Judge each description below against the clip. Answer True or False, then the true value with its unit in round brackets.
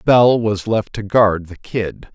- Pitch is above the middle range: False (105 Hz)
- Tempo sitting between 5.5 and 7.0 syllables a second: False (3.5 syllables/s)